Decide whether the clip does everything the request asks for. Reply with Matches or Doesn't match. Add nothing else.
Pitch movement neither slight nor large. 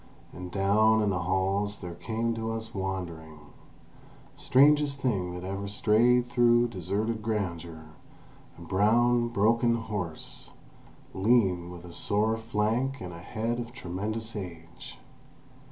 Matches